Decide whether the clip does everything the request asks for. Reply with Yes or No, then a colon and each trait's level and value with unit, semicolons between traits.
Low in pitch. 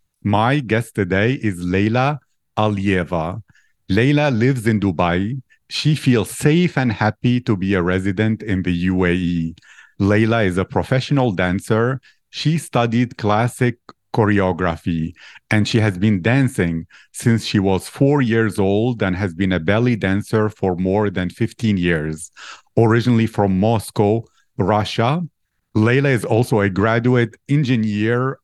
Yes: low, 110 Hz